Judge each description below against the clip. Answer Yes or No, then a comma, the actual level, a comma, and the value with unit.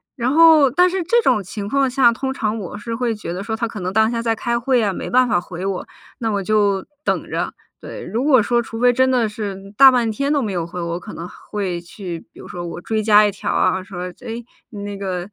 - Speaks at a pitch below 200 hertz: No, high, 220 Hz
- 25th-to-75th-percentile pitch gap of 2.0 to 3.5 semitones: No, average, 4.2 semitones